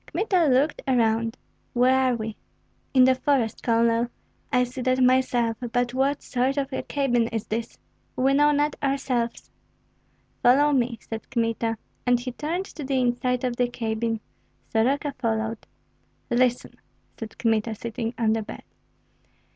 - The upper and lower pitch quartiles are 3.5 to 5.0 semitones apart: No, narrow, 2.5 semitones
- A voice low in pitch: No, high, 245 Hz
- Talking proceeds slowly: No, average, 145 wpm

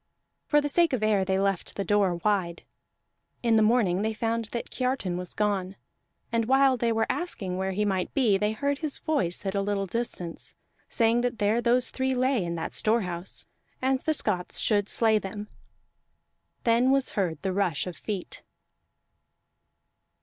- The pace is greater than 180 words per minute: No, average, 170 wpm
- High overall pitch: Yes, high, 215 Hz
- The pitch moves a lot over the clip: No, average, 4.3 semitones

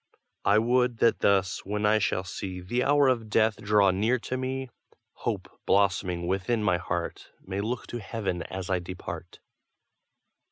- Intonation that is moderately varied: Yes, average, 4.1 semitones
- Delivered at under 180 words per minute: Yes, average, 160 wpm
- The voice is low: Yes, low, 105 Hz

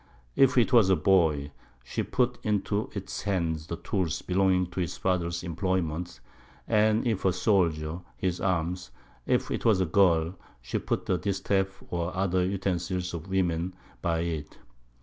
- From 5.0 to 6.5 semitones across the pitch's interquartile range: No, narrow, 2.4 semitones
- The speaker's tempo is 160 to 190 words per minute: No, average, 150 wpm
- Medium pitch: No, very low, 90 Hz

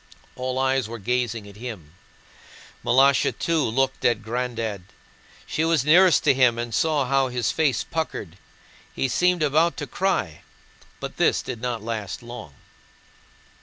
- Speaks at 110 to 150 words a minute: Yes, average, 145 wpm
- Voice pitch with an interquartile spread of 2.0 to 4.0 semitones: Yes, average, 3.6 semitones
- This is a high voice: No, low, 125 Hz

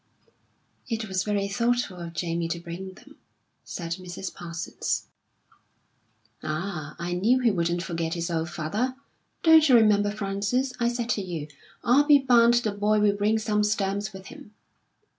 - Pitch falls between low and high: No, high, 200 Hz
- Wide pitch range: No, average, 4.9 semitones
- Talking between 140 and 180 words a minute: Yes, average, 160 wpm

